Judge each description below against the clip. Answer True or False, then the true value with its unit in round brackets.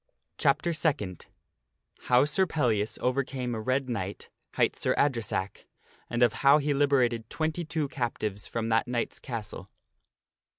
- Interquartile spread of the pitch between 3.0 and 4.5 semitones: True (4.2 semitones)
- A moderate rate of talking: False (130 wpm)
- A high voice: False (125 Hz)